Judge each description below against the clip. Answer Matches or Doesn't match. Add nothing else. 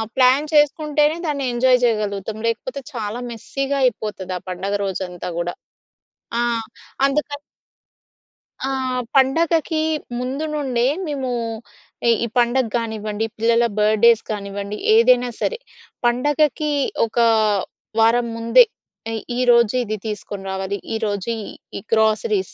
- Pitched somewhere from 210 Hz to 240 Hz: Matches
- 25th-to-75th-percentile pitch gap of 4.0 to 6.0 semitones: Matches